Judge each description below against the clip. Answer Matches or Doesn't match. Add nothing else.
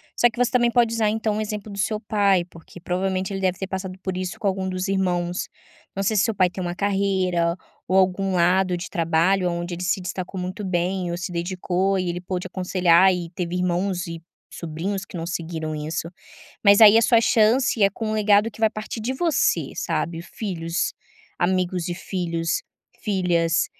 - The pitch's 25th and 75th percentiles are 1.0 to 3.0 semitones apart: Matches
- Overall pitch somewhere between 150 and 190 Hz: Matches